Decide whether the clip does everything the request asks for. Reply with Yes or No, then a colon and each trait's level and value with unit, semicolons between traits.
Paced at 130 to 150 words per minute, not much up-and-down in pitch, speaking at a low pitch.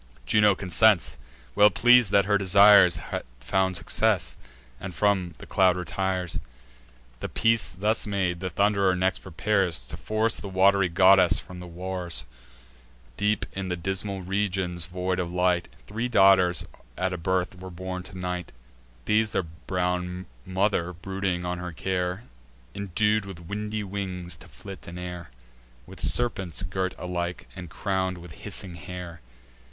Yes: average, 145 wpm; narrow, 1.9 semitones; very low, 95 Hz